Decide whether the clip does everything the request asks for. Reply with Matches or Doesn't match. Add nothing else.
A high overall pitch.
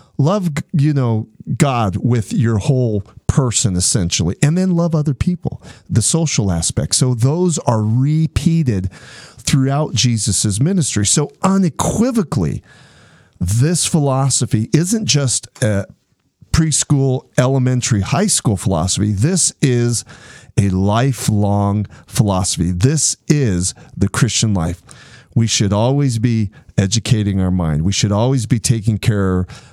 Doesn't match